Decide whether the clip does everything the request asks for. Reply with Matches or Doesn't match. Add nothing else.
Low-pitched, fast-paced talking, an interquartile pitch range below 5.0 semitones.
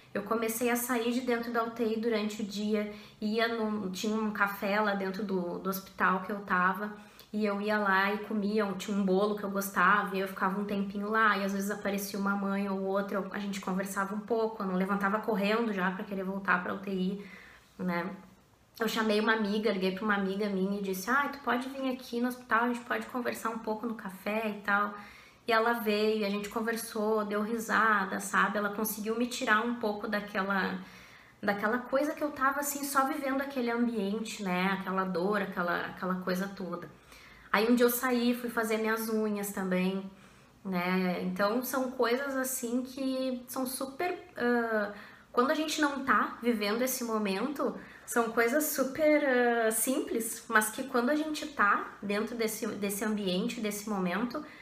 Doesn't match